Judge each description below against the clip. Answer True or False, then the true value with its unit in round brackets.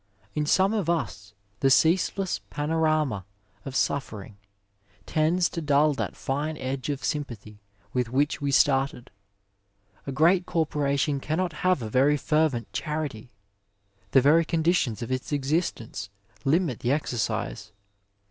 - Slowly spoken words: True (130 wpm)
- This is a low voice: False (145 Hz)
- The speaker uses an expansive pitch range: False (3.6 semitones)